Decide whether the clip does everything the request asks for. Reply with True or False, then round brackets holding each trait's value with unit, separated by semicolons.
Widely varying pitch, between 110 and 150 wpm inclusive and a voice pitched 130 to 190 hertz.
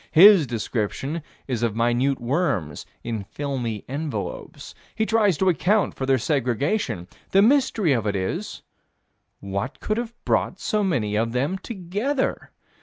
True (8.9 semitones; 140 wpm; 140 Hz)